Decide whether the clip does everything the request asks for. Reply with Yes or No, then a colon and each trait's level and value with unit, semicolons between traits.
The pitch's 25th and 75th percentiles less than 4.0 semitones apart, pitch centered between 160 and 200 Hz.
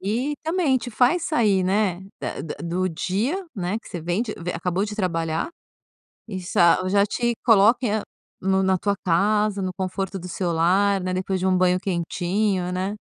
Yes: average, 2.8 semitones; high, 190 Hz